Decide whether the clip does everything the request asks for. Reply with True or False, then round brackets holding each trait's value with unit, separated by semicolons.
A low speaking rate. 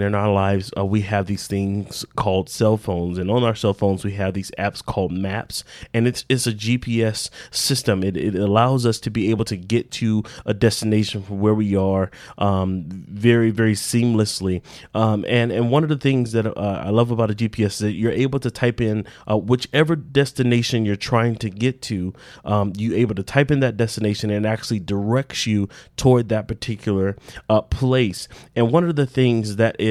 False (205 wpm)